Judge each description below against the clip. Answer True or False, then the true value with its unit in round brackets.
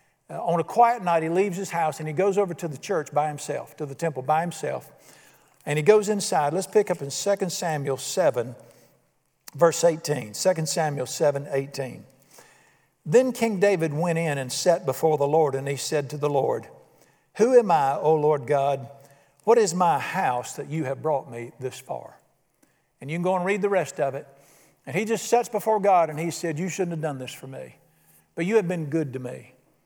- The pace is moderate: False (210 wpm)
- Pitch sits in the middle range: True (160 Hz)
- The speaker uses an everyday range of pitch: True (5.0 semitones)